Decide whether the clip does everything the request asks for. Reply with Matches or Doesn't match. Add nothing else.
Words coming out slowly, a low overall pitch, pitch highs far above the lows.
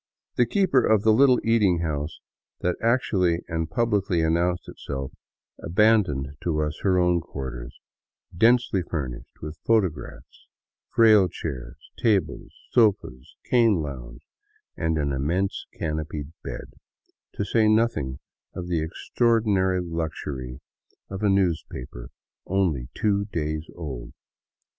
Matches